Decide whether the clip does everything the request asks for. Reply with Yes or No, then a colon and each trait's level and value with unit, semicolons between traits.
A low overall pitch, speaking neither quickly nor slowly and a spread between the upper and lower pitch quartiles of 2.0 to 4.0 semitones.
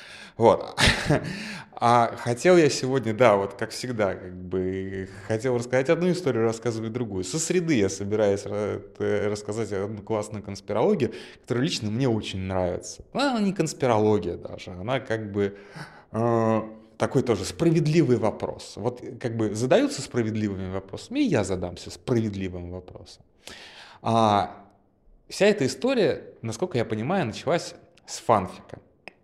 Yes: low, 110 Hz; average, 130 wpm; average, 3.6 semitones